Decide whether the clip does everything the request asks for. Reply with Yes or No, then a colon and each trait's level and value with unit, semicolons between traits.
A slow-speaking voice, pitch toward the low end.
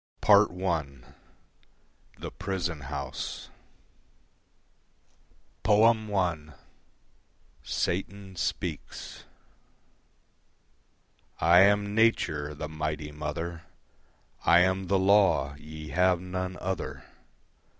Yes: slow, 75 wpm; very low, 90 Hz